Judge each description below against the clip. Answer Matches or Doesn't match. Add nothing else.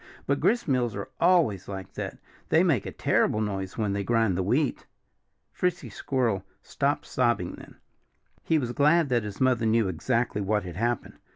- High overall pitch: Doesn't match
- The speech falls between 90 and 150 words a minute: Doesn't match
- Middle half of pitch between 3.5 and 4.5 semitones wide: Doesn't match